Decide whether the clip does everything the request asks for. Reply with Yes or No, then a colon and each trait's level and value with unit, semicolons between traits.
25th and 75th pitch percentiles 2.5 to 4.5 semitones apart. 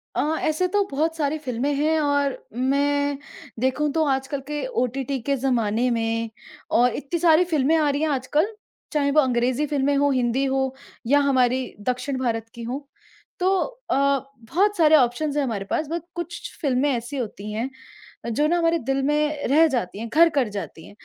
Yes: average, 3.5 semitones